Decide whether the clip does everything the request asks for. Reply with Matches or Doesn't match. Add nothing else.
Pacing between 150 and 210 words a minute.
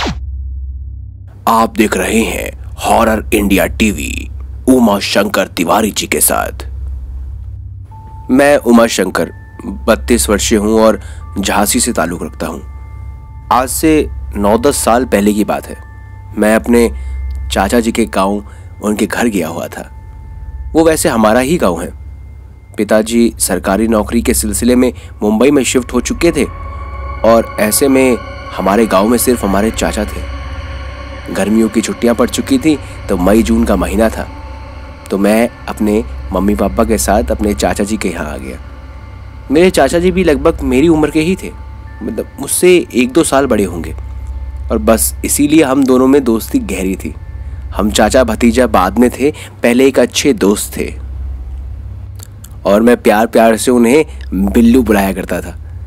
Matches